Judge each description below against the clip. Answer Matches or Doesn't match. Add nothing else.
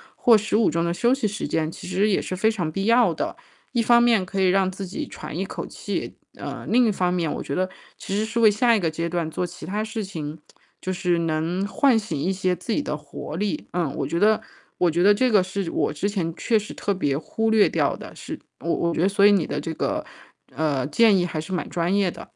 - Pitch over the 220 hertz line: Doesn't match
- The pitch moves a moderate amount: Matches